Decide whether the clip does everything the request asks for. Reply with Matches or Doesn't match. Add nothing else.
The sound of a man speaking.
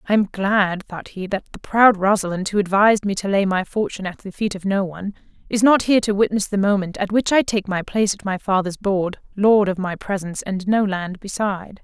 Doesn't match